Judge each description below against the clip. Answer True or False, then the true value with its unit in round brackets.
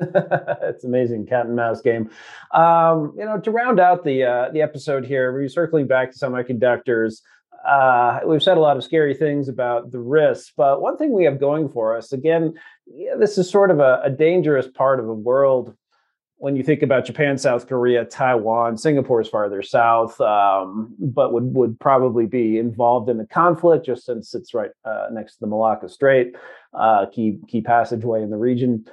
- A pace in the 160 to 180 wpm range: False (190 wpm)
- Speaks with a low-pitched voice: True (130 Hz)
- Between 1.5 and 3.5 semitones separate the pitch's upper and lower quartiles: False (4.7 semitones)